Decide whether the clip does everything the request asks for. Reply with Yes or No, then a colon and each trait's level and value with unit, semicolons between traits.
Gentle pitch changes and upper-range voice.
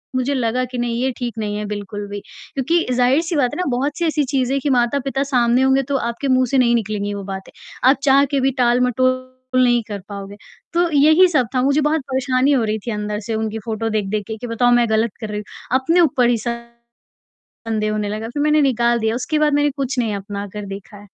No: average, 3.8 semitones; high, 245 Hz